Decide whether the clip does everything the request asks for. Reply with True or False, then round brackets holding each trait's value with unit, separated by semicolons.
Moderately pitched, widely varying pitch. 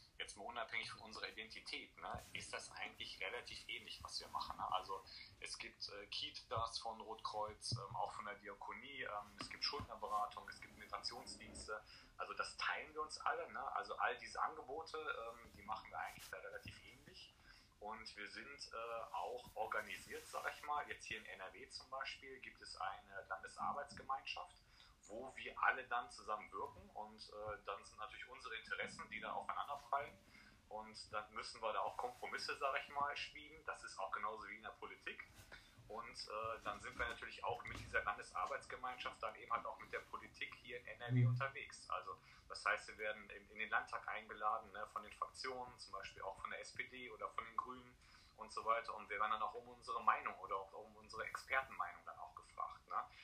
False (130 Hz; 6.3 semitones)